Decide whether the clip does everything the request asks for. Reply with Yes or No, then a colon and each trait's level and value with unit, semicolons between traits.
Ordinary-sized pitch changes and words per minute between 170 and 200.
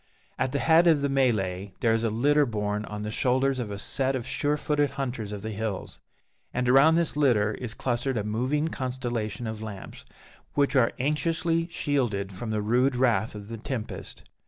Yes: average, 4.5 semitones; average, 190 wpm